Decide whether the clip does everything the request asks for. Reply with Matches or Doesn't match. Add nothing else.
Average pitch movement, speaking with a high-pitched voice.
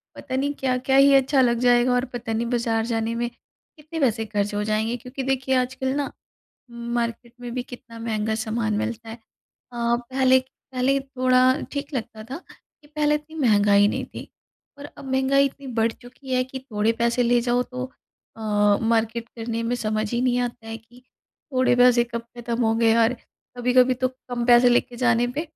Doesn't match